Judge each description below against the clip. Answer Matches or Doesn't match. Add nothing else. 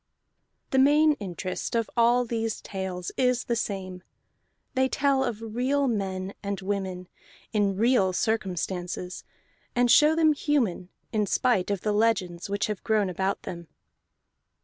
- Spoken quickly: Doesn't match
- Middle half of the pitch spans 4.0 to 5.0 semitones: Matches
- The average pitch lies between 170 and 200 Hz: Doesn't match